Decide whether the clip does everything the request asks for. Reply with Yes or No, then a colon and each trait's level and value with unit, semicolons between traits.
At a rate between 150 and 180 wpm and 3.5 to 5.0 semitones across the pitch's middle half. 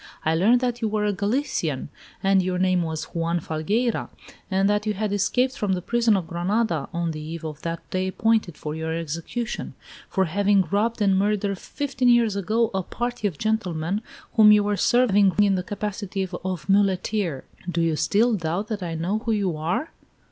No: average, 190 wpm; average, 4.0 semitones